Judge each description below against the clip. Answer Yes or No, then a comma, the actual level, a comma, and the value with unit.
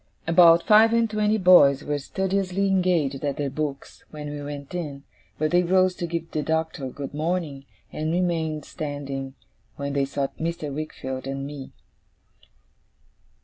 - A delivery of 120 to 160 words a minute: Yes, average, 150 wpm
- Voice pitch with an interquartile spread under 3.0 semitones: No, average, 4.0 semitones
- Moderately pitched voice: Yes, medium, 155 Hz